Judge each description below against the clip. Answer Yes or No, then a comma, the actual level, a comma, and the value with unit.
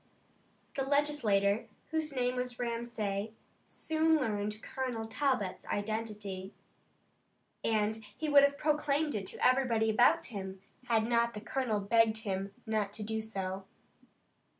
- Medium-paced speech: No, slow, 125 wpm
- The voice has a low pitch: No, high, 225 Hz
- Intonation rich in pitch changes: No, average, 4.0 semitones